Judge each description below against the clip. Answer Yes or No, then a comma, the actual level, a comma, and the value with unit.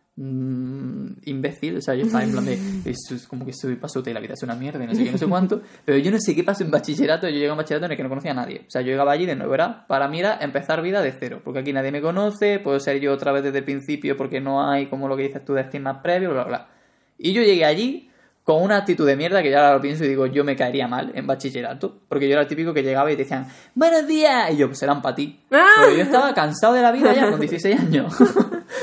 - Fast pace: Yes, fast, 285 wpm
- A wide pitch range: Yes, wide, 6.5 semitones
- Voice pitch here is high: No, medium, 145 Hz